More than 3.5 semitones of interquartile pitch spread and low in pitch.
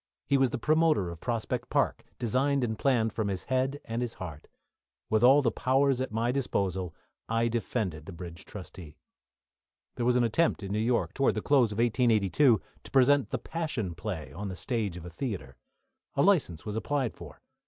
Yes: wide, 5.4 semitones; low, 115 Hz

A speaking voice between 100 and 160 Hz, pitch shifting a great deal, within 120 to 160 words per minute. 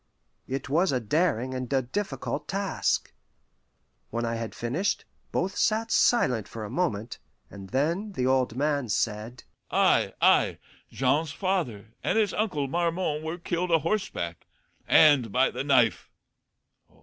Yes: medium, 140 Hz; wide, 7.0 semitones; average, 140 wpm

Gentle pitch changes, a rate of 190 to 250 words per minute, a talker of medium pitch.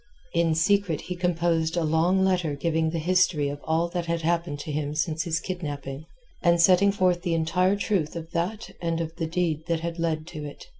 Yes: narrow, 2.0 semitones; fast, 205 wpm; medium, 165 Hz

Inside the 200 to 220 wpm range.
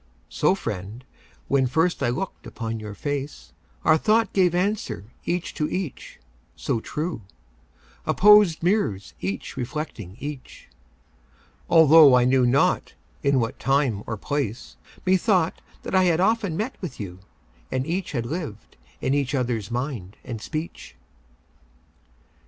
No: slow, 135 wpm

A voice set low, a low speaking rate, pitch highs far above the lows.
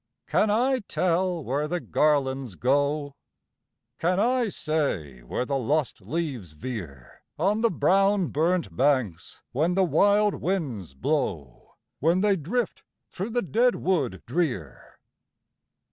No: medium, 155 Hz; slow, 125 wpm; wide, 6.9 semitones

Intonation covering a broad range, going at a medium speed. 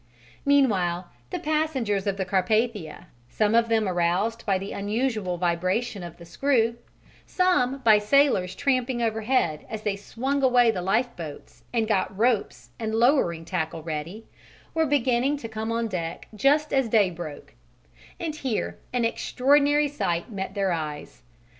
Yes: wide, 5.7 semitones; average, 145 wpm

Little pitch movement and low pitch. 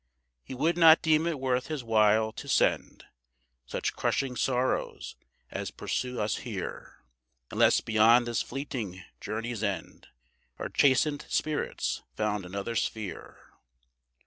No: average, 4.2 semitones; low, 120 Hz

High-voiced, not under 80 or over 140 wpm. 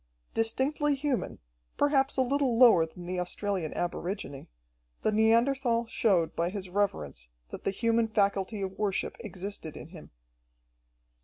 Yes: high, 205 Hz; slow, 135 wpm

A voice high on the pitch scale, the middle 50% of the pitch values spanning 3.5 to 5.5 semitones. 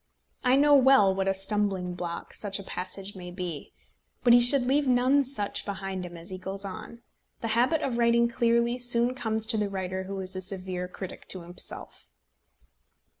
Yes: high, 200 Hz; average, 4.3 semitones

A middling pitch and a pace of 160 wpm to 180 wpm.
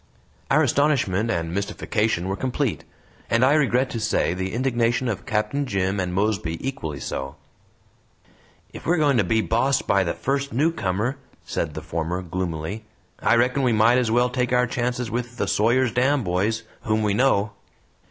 No: low, 115 Hz; average, 170 wpm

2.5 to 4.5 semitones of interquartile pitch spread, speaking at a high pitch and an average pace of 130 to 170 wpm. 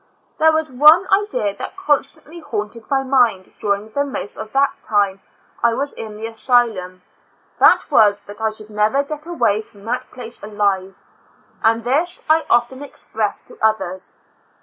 No: average, 5.1 semitones; high, 225 Hz; average, 165 wpm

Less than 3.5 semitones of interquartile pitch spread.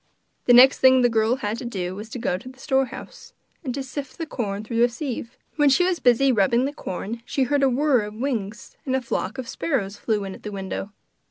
No: average, 4.0 semitones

